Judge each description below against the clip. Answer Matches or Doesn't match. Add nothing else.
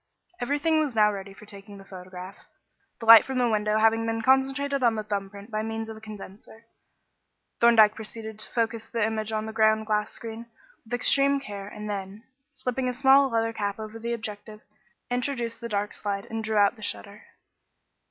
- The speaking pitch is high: Matches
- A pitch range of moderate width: Doesn't match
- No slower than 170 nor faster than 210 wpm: Matches